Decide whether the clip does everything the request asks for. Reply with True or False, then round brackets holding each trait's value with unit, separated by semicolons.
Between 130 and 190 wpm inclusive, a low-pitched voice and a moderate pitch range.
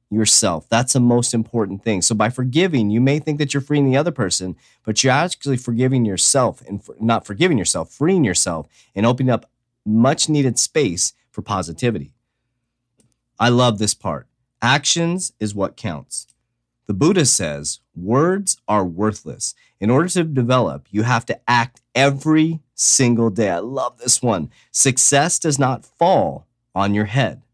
True (160 wpm; 120 Hz; 4.1 semitones)